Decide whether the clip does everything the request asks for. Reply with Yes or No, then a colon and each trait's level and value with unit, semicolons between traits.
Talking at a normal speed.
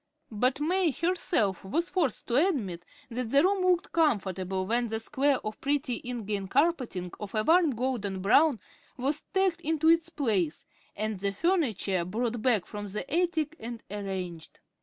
Yes: average, 160 wpm